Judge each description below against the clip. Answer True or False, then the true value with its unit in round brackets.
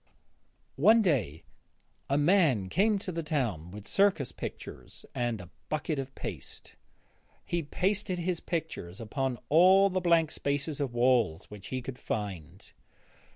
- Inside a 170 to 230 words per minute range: False (140 wpm)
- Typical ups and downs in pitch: False (7.5 semitones)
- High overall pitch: False (140 Hz)